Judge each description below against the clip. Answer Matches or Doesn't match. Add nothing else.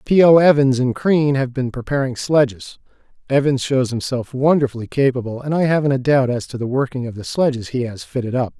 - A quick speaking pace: Matches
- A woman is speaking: Doesn't match